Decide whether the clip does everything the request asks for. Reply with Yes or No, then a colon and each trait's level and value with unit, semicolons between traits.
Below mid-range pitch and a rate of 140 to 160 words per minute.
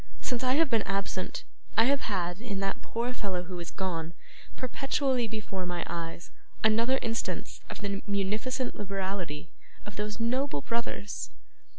No: high, 205 Hz; average, 150 wpm